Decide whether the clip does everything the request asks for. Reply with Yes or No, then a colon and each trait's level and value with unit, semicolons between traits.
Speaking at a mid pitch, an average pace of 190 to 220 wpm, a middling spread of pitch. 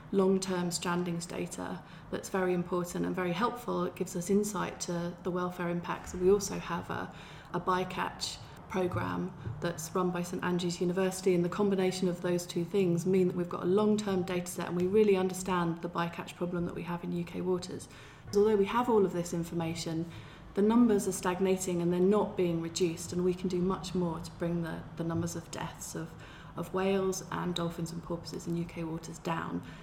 No: medium, 180 Hz; average, 200 wpm; narrow, 1.7 semitones